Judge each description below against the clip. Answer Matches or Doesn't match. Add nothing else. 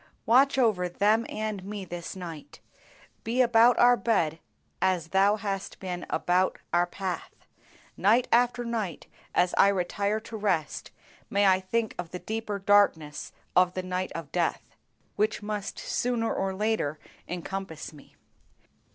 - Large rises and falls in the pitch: Doesn't match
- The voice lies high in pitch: Matches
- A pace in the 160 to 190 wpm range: Doesn't match